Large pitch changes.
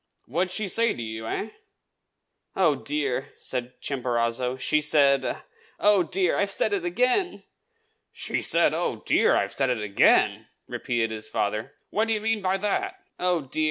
Yes: wide, 8.1 semitones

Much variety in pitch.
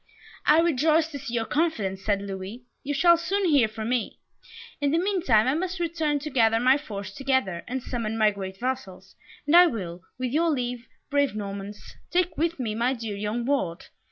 Yes: wide, 6.5 semitones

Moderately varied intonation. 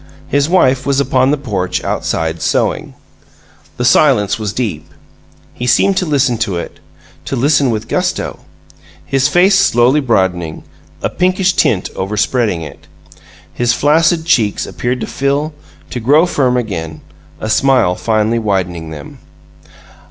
No: wide, 6.0 semitones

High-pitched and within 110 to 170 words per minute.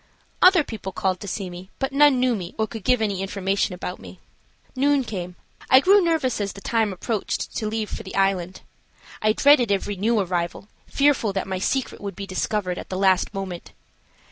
No: high, 200 Hz; average, 195 wpm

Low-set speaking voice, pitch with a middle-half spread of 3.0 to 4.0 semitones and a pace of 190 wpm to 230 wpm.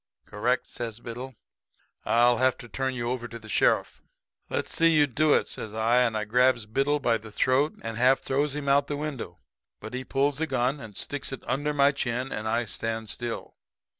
Yes: low, 125 Hz; average, 3.4 semitones; fast, 205 wpm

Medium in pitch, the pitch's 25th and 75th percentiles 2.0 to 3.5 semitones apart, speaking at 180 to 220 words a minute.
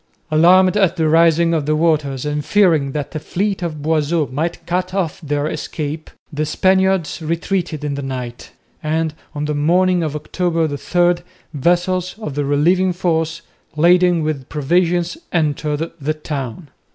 No: medium, 160 Hz; average, 3.0 semitones; average, 155 wpm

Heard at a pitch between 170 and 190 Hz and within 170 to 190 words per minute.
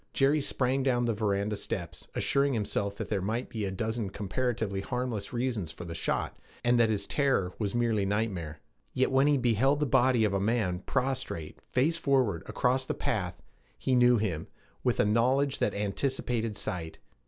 No: low, 115 Hz; average, 175 wpm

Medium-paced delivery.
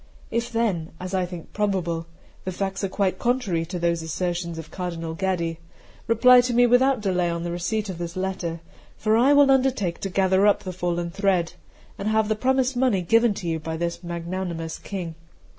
Yes: average, 190 wpm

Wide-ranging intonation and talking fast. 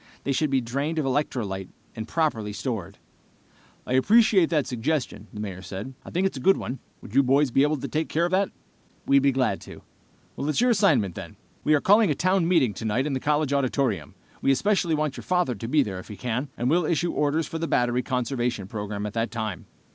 Yes: wide, 5.8 semitones; fast, 225 wpm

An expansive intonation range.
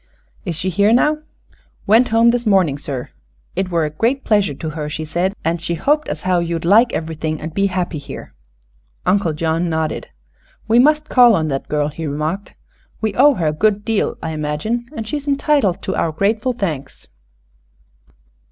Yes: wide, 6.2 semitones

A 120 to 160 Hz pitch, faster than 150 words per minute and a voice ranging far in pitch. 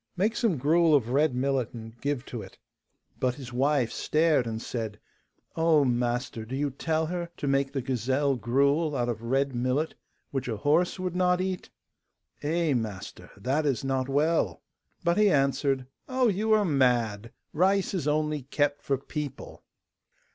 No: medium, 140 Hz; average, 165 wpm; average, 4.3 semitones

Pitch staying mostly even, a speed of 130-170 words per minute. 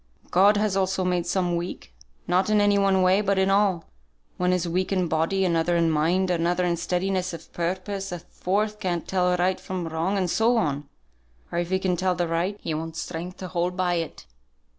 No: narrow, 1.9 semitones; fast, 205 wpm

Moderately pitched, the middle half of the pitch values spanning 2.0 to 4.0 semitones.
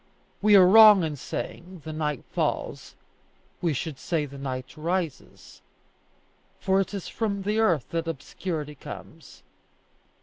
No: medium, 165 Hz; average, 4.5 semitones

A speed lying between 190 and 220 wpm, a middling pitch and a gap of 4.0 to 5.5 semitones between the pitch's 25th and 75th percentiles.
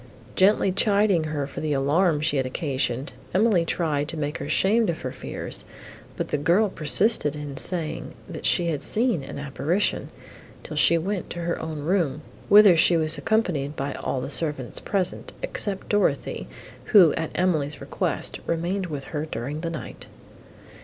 No: average, 165 wpm; medium, 160 Hz; average, 4.4 semitones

